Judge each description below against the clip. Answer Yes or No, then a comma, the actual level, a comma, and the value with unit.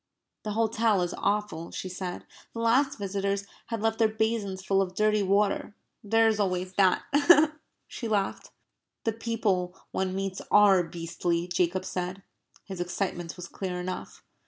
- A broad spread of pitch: No, average, 2.8 semitones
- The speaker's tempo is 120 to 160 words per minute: Yes, average, 150 wpm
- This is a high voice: Yes, high, 195 Hz